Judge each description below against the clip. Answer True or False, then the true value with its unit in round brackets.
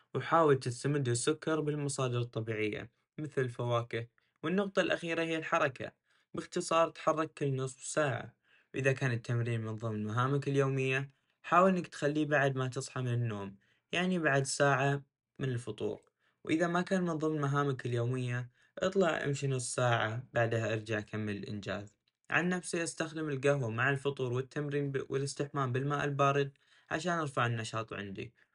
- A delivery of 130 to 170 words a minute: True (135 wpm)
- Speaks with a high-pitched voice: False (140 Hz)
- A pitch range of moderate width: True (4.2 semitones)